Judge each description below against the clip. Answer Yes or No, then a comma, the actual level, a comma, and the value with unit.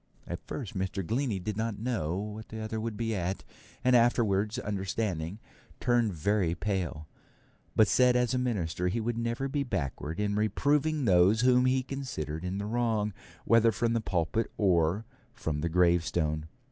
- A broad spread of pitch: No, average, 4.7 semitones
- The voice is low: Yes, low, 105 Hz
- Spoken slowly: No, average, 165 wpm